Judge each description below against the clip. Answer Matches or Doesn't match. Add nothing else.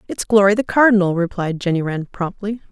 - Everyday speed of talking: Matches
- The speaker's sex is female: Matches